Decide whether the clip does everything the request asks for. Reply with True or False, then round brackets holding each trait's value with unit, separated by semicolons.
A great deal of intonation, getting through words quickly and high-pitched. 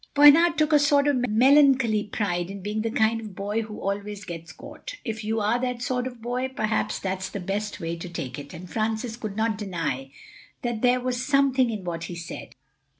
False (4.3 semitones; 210 wpm; 220 Hz)